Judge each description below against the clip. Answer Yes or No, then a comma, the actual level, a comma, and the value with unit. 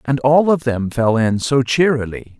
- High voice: No, low, 130 Hz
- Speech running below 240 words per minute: Yes, average, 200 wpm